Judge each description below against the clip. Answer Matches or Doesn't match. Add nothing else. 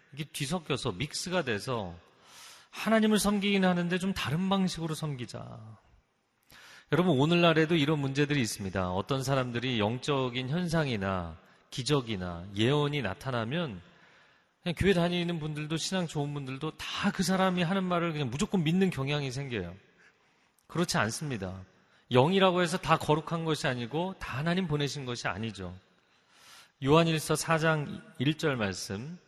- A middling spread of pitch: Doesn't match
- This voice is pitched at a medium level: Matches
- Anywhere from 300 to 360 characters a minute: Matches